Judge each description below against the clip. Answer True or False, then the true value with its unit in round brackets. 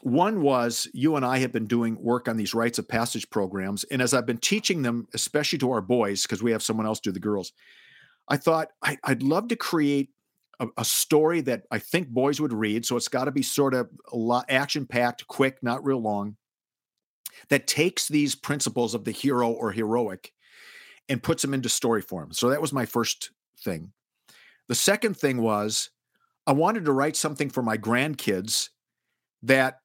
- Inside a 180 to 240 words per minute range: True (195 wpm)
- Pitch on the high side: False (125 Hz)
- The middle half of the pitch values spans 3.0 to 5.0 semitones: True (3.8 semitones)